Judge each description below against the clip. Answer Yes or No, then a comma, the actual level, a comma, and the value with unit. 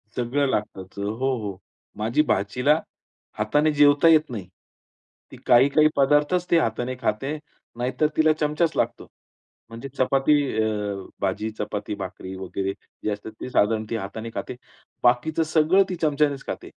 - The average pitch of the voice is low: Yes, low, 125 Hz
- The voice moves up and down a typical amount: No, wide, 6.0 semitones